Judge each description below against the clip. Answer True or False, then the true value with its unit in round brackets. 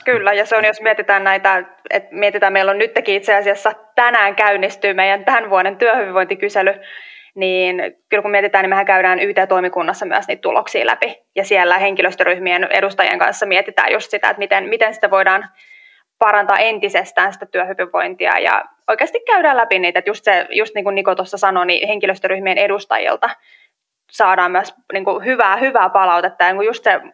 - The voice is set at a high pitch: True (200 Hz)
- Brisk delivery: True (170 wpm)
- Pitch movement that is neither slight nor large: False (1.9 semitones)